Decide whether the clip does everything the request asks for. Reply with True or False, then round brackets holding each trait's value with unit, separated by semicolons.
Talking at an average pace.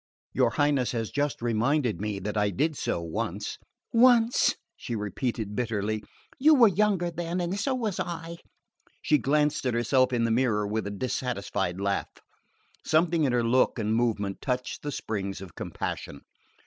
True (165 wpm)